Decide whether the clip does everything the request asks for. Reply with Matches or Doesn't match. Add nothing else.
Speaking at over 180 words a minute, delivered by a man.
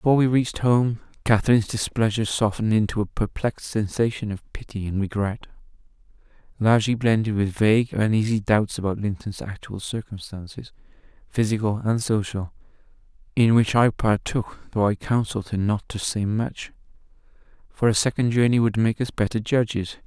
Doesn't match